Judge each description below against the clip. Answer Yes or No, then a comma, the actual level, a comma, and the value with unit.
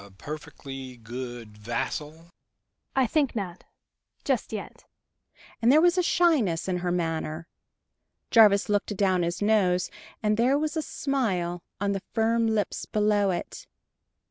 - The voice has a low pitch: No, high, 195 Hz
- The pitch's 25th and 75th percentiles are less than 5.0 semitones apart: No, wide, 5.6 semitones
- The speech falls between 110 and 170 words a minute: Yes, slow, 135 wpm